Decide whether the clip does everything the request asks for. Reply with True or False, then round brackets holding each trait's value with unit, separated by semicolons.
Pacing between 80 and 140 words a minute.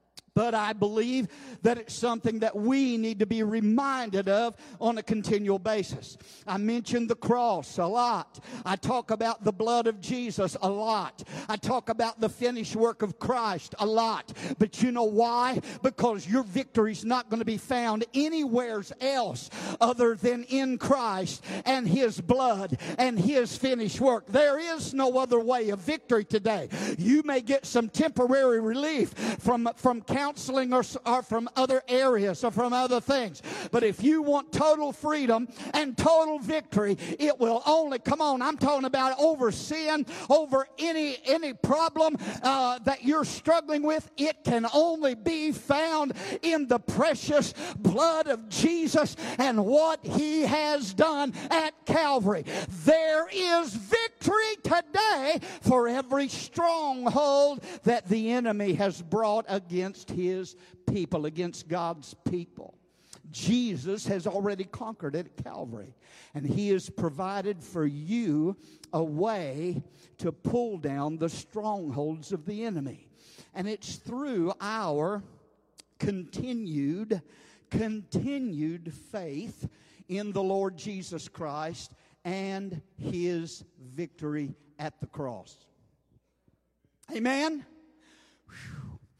True (135 wpm)